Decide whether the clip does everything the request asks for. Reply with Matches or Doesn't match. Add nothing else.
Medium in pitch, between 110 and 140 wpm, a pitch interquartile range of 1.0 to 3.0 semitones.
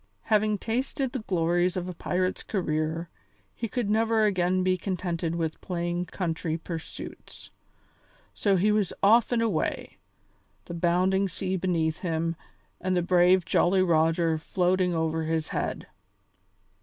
Matches